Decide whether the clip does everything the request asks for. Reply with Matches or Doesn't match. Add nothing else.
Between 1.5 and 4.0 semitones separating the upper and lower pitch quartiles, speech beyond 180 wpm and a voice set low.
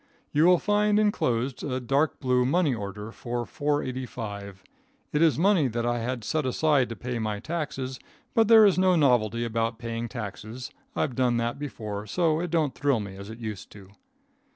Doesn't match